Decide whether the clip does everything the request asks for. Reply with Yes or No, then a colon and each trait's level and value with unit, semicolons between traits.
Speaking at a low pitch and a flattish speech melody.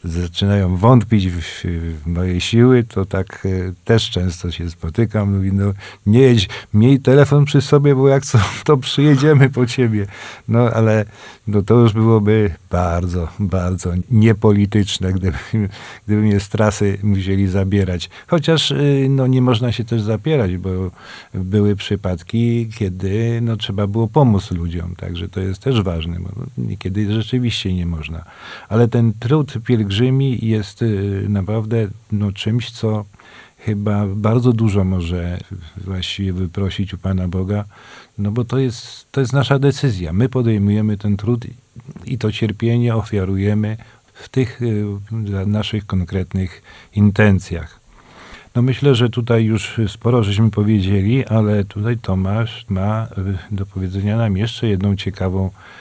No: low, 105 Hz; average, 3.5 semitones